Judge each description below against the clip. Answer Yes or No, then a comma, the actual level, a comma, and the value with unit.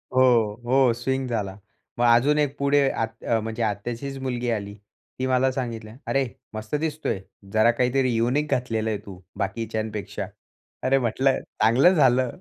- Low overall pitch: Yes, low, 120 Hz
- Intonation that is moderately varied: Yes, average, 3.1 semitones